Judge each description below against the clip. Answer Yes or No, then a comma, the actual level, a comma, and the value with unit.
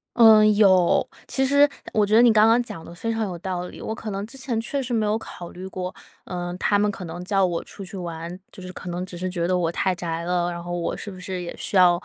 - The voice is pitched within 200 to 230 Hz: No, medium, 185 Hz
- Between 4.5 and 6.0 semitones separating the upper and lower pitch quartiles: No, average, 3.5 semitones